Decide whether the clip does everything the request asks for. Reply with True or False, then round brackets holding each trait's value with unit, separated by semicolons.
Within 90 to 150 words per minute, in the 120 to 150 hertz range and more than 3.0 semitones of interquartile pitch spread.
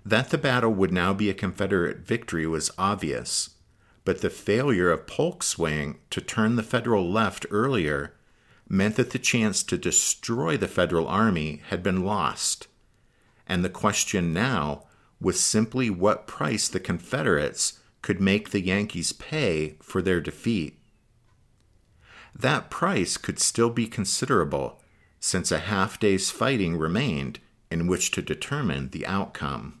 False (140 wpm; 100 Hz; 4.1 semitones)